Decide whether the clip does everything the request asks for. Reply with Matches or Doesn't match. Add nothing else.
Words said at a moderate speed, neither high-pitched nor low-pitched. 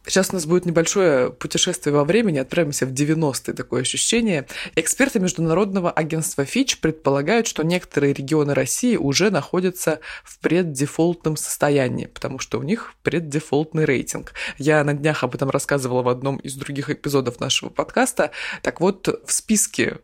Matches